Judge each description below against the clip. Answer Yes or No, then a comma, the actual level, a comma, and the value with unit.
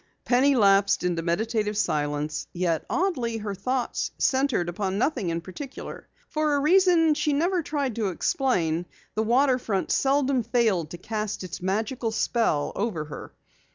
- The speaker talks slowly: No, average, 145 wpm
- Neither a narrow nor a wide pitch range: No, wide, 6.8 semitones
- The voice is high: Yes, high, 220 Hz